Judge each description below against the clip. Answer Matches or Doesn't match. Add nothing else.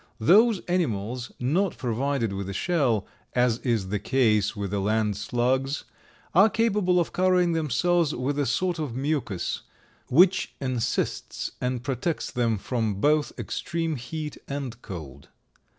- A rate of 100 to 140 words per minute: Matches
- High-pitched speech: Doesn't match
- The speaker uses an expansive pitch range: Matches